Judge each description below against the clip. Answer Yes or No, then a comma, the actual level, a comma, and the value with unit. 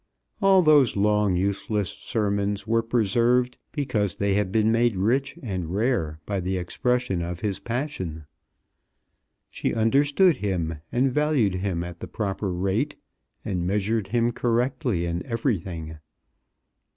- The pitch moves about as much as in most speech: Yes, average, 4.8 semitones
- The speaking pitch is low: Yes, low, 105 Hz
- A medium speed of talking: No, slow, 130 wpm